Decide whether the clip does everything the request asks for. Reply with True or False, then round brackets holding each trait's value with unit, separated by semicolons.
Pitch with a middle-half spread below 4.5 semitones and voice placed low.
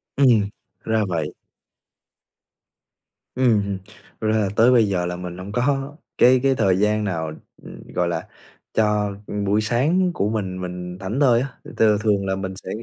True (4.1 semitones; 105 Hz)